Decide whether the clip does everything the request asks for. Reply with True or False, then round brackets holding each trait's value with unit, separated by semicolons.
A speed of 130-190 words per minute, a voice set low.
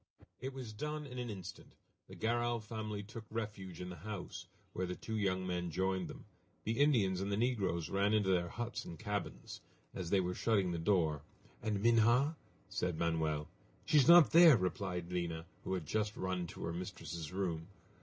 True (185 wpm; 100 Hz)